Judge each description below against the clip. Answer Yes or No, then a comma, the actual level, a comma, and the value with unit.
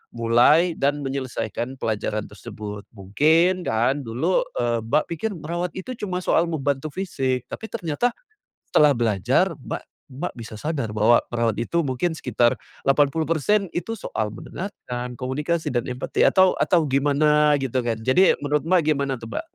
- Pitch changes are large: Yes, wide, 5.9 semitones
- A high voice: No, medium, 140 Hz